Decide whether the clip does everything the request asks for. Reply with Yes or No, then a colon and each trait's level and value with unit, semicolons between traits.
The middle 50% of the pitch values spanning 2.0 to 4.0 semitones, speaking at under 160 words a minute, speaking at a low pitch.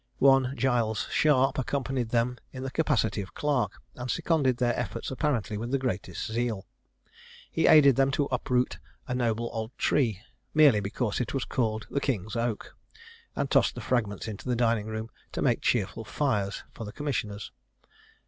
No: average, 3.4 semitones; average, 165 wpm; low, 120 Hz